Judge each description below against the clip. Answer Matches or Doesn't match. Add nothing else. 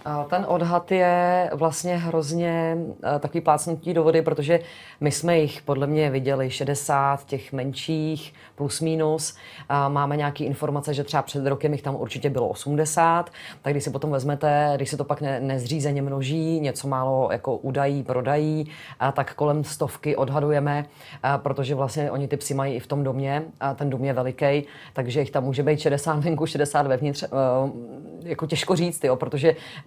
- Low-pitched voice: Doesn't match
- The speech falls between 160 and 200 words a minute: Matches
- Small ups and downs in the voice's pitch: Matches